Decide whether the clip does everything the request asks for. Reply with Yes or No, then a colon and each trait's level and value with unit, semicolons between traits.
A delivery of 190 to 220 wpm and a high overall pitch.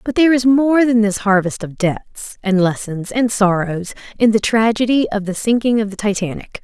Yes: average, 200 wpm; high, 215 Hz